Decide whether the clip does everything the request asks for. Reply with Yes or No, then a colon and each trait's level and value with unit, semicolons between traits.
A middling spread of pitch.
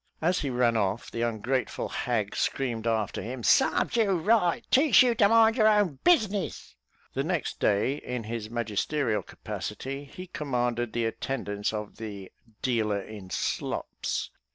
No: wide, 8.4 semitones